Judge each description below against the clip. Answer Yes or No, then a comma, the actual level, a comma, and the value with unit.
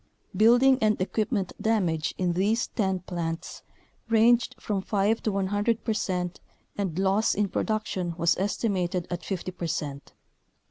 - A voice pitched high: Yes, high, 195 Hz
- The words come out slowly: Yes, slow, 130 wpm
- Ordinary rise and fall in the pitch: Yes, average, 3.4 semitones